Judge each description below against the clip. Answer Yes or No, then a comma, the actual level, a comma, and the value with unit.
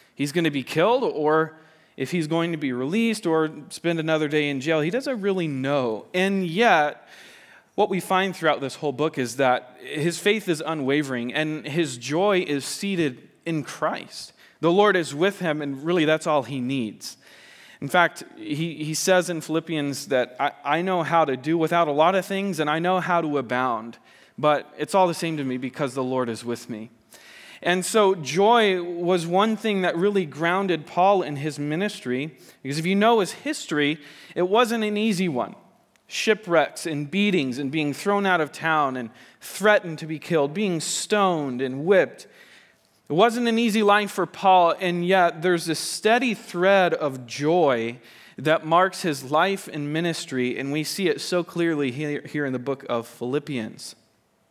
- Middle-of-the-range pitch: Yes, medium, 160 Hz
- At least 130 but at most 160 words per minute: No, average, 185 wpm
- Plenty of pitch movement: No, average, 4.3 semitones